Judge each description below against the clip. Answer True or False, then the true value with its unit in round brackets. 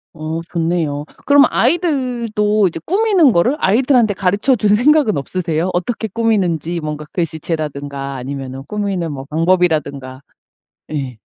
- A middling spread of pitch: False (6.9 semitones)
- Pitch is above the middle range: False (180 Hz)